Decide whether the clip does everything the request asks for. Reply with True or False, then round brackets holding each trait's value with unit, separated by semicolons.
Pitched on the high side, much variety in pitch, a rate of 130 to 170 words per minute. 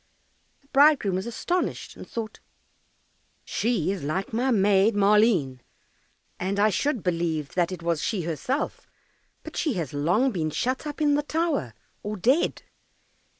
True (205 Hz; 7.2 semitones; 150 wpm)